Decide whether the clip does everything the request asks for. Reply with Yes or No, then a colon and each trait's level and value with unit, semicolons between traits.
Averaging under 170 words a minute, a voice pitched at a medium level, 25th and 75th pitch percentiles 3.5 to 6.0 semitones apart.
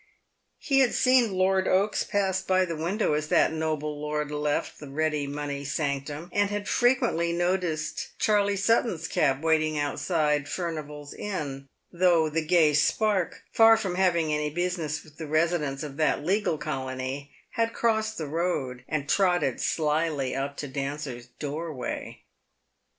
Yes: average, 145 wpm; medium, 155 Hz; average, 4.1 semitones